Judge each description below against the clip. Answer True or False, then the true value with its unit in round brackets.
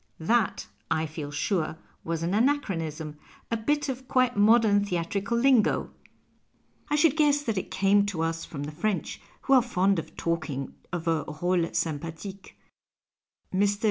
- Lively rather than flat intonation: True (6.2 semitones)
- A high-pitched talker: True (195 Hz)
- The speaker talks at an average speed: True (155 wpm)